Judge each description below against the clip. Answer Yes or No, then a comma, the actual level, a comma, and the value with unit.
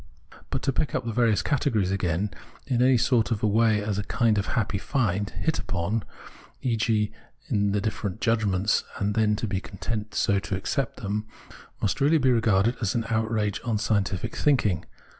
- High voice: No, low, 110 Hz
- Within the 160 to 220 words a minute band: Yes, average, 180 wpm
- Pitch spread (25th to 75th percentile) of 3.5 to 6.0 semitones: No, narrow, 2.6 semitones